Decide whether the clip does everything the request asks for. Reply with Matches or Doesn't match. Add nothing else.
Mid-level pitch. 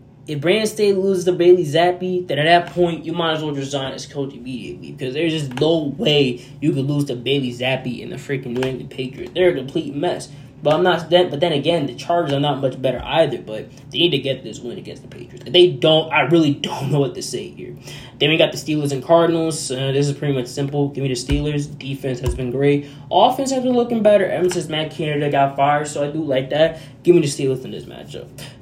Matches